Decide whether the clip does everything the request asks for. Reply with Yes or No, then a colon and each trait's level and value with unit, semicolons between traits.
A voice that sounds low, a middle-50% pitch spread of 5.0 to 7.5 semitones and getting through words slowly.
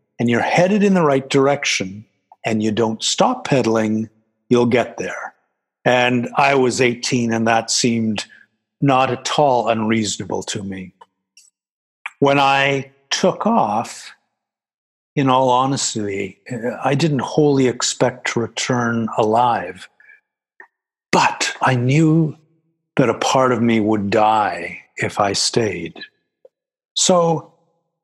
Yes: low, 130 Hz; wide, 5.6 semitones; slow, 120 wpm